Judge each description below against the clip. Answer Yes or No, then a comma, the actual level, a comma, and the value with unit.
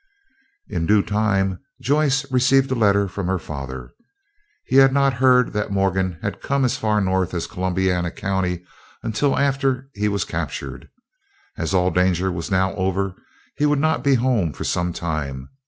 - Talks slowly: No, average, 165 wpm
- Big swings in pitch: Yes, wide, 6.2 semitones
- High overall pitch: No, low, 100 Hz